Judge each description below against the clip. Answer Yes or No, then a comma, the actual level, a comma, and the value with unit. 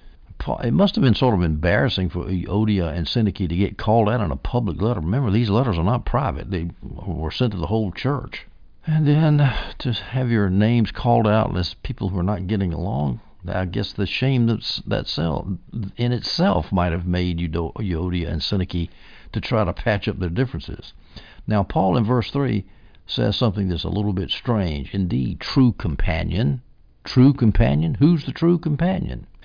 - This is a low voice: Yes, low, 105 Hz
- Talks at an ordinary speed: Yes, average, 180 wpm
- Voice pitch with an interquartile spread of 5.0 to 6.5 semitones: Yes, wide, 5.4 semitones